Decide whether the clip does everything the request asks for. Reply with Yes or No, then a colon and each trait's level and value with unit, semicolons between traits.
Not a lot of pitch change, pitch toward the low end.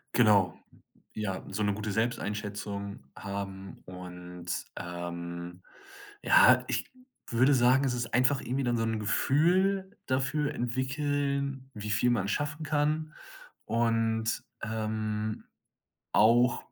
No: average, 4.9 semitones; low, 115 Hz